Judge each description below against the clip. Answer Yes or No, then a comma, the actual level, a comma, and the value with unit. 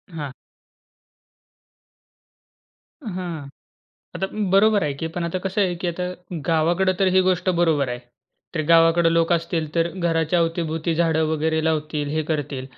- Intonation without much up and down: Yes, narrow, 2.2 semitones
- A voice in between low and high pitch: Yes, medium, 165 Hz